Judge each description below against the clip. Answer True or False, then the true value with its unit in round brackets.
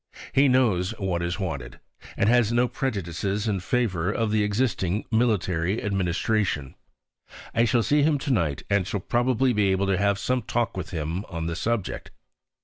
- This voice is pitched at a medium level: False (100 Hz)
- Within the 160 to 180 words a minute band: True (170 wpm)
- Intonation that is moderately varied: True (4.7 semitones)